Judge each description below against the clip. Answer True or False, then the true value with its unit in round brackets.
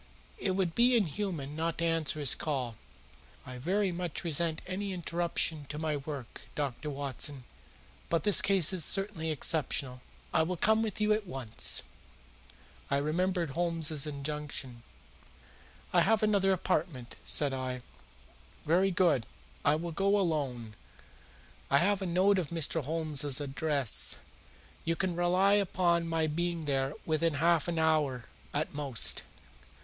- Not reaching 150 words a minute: True (140 wpm)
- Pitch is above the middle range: False (160 Hz)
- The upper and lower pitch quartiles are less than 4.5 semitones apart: True (4.0 semitones)